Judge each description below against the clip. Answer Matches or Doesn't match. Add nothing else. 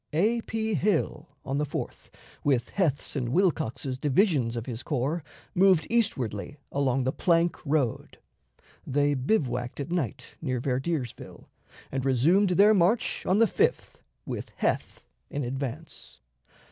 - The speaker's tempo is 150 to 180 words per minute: Doesn't match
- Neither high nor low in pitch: Matches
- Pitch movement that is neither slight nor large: Doesn't match